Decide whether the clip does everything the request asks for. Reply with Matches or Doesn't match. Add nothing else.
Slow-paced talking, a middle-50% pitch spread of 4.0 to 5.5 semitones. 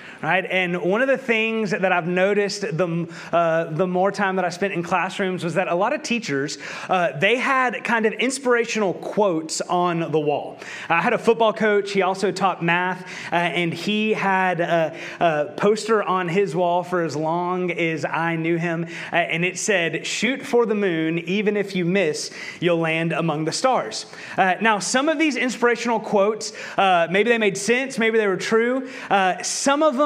Doesn't match